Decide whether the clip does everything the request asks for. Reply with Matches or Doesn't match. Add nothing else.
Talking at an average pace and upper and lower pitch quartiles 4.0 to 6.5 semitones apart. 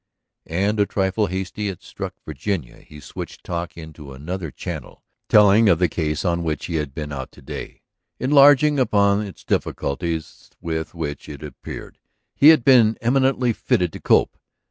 Matches